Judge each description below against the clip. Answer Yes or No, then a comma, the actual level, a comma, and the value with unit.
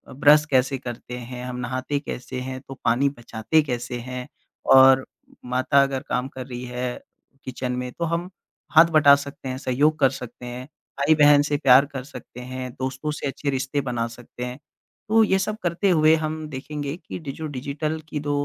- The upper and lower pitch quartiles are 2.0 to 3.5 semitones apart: Yes, average, 2.9 semitones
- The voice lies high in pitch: No, low, 135 Hz